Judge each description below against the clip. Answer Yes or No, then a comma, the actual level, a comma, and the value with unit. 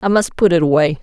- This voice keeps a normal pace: No, fast, 290 wpm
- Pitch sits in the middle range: Yes, medium, 175 Hz